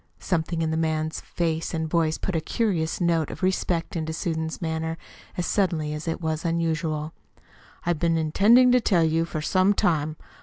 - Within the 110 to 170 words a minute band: No, average, 180 wpm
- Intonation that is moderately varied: No, narrow, 1.6 semitones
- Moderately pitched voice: Yes, medium, 165 Hz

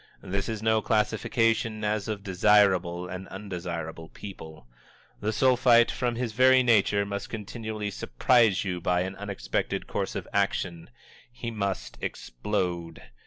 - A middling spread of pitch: Yes, average, 3.4 semitones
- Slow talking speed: Yes, slow, 130 wpm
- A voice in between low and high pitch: No, low, 100 Hz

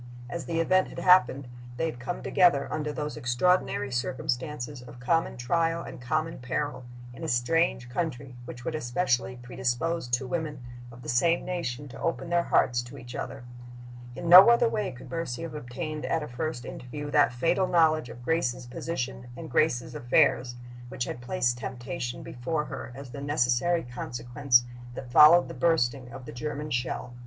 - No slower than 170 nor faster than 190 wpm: Yes, average, 175 wpm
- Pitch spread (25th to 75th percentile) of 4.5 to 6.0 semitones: Yes, average, 5.1 semitones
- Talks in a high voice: No, low, 135 Hz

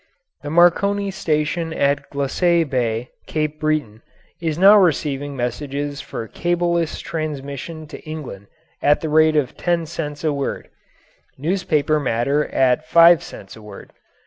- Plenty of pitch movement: No, average, 3.1 semitones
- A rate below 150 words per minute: Yes, slow, 135 wpm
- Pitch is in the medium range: Yes, medium, 150 Hz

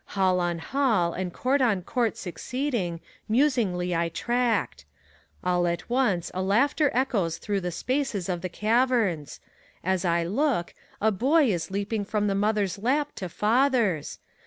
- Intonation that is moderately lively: No, wide, 5.9 semitones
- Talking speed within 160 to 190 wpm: No, average, 150 wpm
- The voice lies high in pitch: Yes, high, 205 Hz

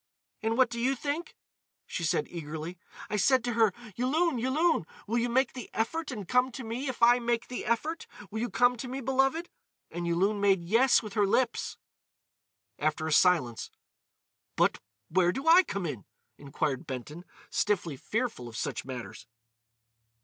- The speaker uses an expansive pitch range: Yes, wide, 7.1 semitones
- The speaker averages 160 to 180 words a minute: Yes, average, 165 wpm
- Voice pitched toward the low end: No, high, 225 Hz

